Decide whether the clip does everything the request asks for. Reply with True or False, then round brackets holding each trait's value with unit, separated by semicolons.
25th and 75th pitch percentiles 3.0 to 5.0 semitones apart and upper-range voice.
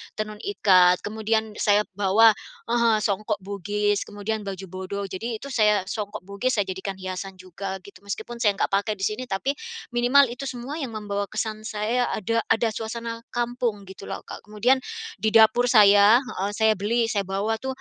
False (2.5 semitones; 215 Hz)